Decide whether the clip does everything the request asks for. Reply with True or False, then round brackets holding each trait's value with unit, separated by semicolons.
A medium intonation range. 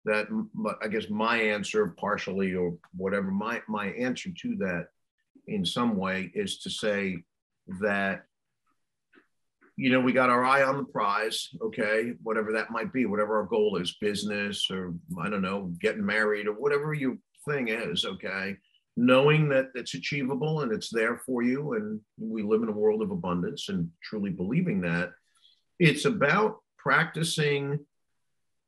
False (8.5 semitones)